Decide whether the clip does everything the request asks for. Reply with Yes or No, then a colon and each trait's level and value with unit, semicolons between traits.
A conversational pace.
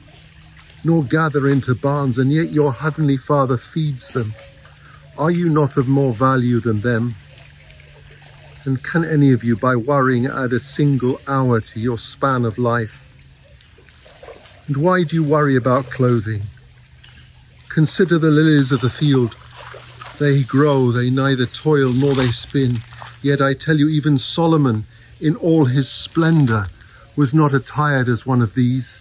Yes: average, 150 wpm